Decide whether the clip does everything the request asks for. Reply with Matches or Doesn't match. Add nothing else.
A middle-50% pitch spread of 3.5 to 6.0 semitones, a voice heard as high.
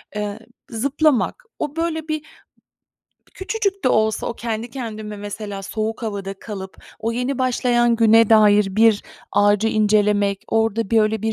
Doesn't match